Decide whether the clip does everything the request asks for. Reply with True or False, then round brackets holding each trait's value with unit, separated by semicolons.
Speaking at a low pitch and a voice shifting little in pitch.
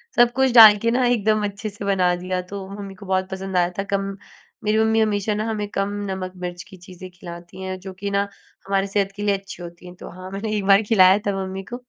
False (195 Hz; 2.0 semitones)